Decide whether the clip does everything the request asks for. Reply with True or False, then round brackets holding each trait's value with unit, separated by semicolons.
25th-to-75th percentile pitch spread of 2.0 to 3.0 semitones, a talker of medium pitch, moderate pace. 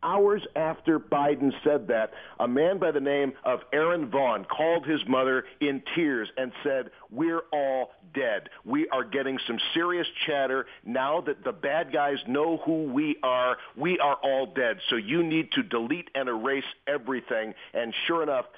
False (3.8 semitones; 145 Hz; 170 wpm)